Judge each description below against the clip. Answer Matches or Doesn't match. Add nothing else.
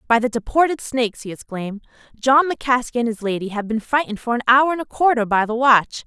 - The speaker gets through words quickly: Matches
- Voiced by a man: Doesn't match